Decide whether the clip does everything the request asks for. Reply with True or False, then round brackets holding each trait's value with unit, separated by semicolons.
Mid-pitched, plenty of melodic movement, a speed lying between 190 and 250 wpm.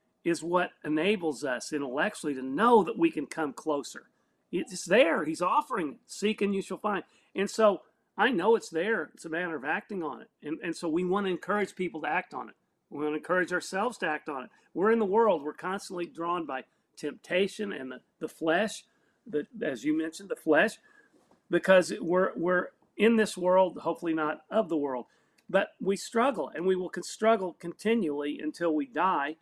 False (180 Hz; 4.4 semitones; 200 wpm)